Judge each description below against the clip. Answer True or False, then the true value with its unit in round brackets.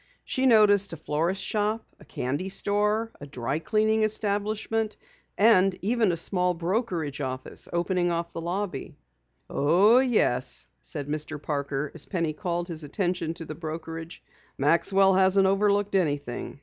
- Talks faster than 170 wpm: False (140 wpm)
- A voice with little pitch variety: False (4.8 semitones)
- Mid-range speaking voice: True (180 Hz)